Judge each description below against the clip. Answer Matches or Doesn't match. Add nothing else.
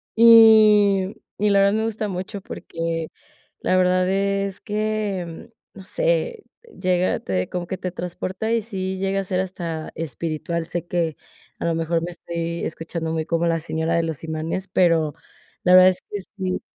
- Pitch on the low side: Doesn't match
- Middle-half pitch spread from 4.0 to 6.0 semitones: Doesn't match